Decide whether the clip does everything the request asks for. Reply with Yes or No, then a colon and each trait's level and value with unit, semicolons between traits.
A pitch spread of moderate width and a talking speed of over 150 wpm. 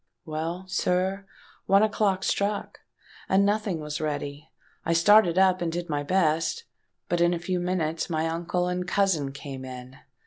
Yes: average, 3.5 semitones; average, 160 wpm